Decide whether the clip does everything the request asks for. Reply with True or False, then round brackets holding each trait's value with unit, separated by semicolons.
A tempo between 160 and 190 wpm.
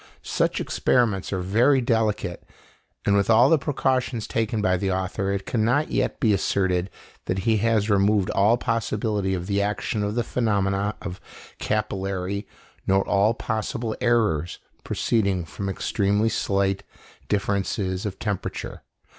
False (140 wpm)